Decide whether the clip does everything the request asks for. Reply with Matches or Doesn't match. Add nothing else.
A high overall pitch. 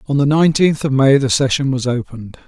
Doesn't match